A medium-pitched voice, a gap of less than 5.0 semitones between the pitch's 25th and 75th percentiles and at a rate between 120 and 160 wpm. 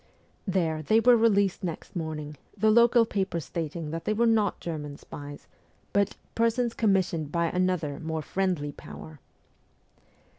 No: medium, 175 Hz; wide, 5.5 semitones; average, 140 wpm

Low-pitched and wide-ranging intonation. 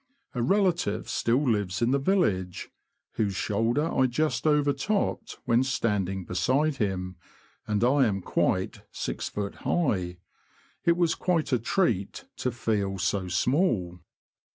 Yes: low, 120 Hz; wide, 7.3 semitones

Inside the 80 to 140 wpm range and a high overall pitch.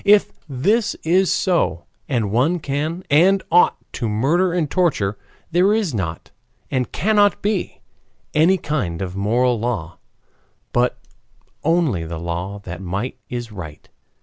No: slow, 135 wpm; low, 130 Hz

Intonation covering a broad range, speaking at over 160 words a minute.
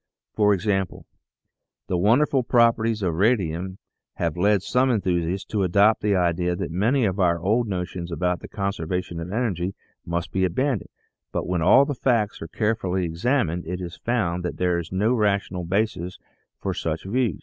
No: average, 4.0 semitones; average, 170 wpm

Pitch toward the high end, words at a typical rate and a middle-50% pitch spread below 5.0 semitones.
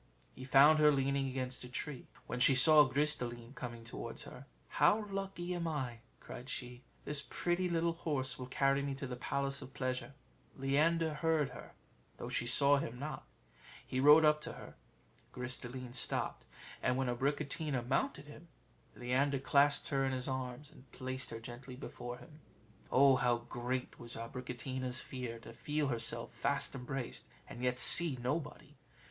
No: low, 135 Hz; average, 170 wpm; average, 2.9 semitones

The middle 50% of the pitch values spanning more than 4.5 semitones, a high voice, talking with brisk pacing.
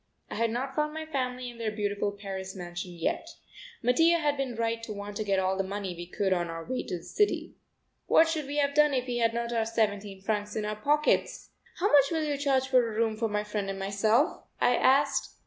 Yes: average, 5.1 semitones; high, 225 Hz; fast, 235 wpm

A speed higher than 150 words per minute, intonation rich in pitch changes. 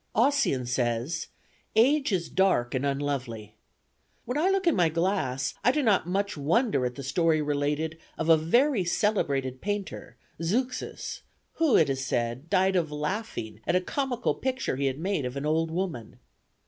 Yes: average, 165 wpm; wide, 7.3 semitones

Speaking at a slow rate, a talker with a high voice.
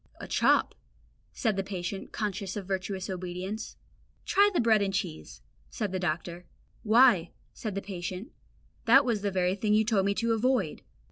No: average, 160 wpm; high, 200 Hz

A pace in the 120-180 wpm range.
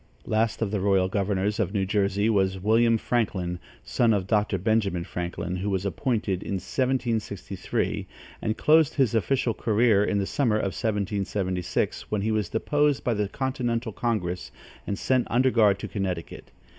Yes: average, 160 wpm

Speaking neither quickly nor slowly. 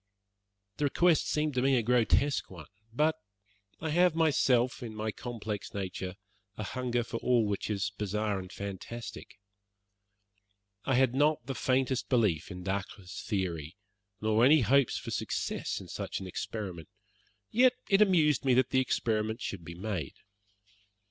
Yes: average, 150 wpm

